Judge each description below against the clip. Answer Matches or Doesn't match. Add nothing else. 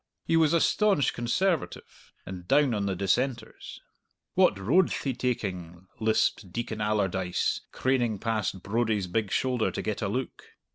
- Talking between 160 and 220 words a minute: Doesn't match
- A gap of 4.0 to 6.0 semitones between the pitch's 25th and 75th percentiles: Matches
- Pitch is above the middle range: Doesn't match